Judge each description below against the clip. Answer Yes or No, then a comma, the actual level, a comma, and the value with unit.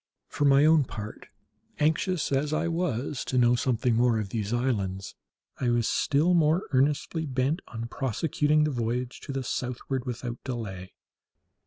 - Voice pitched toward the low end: Yes, low, 130 Hz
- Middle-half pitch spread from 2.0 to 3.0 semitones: No, average, 4.1 semitones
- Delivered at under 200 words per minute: Yes, average, 155 wpm